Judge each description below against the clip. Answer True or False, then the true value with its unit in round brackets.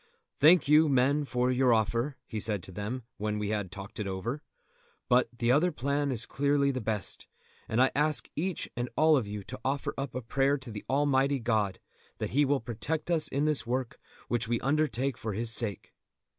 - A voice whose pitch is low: True (125 Hz)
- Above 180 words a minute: True (200 wpm)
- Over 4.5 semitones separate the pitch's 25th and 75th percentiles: False (4.2 semitones)